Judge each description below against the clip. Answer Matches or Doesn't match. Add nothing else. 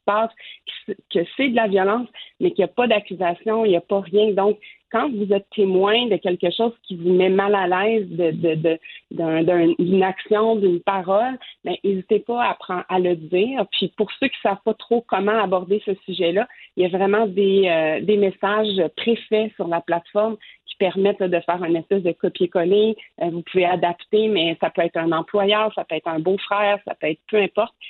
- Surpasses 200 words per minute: Matches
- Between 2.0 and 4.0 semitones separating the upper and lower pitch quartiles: Matches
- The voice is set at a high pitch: Matches